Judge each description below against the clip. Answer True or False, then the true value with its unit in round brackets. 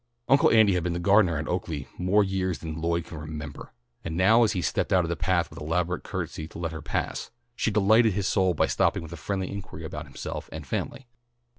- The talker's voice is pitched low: True (90 Hz)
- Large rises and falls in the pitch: False (3.5 semitones)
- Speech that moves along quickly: True (230 wpm)